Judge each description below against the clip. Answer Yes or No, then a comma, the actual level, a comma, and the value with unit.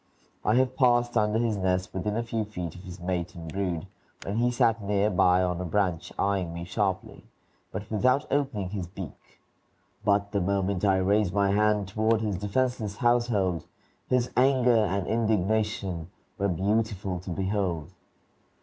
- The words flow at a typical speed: Yes, average, 160 wpm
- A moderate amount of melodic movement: Yes, average, 3.1 semitones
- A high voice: No, low, 100 Hz